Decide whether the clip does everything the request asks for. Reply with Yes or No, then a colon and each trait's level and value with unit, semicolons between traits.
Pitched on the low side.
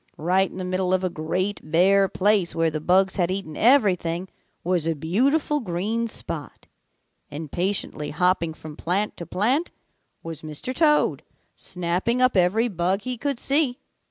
No: medium, 185 Hz